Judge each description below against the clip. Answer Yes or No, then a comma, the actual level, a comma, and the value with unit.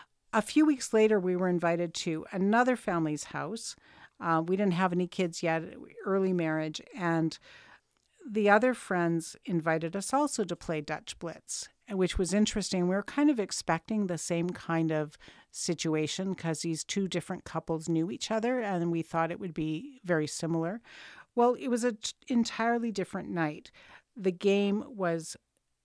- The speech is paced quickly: No, average, 165 wpm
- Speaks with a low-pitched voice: No, medium, 185 Hz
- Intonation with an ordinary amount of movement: Yes, average, 4.7 semitones